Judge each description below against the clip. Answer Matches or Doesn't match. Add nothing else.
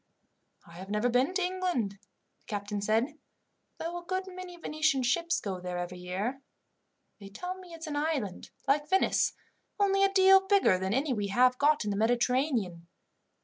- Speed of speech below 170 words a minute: Doesn't match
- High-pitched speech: Matches